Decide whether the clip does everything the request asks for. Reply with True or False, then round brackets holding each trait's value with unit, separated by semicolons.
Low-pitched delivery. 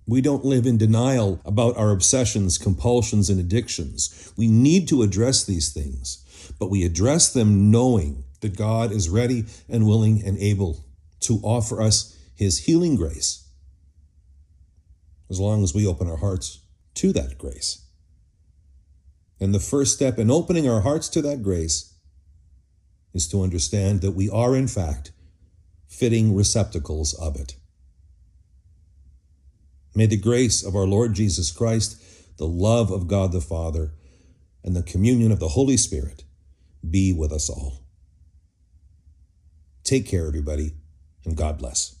True (90 Hz)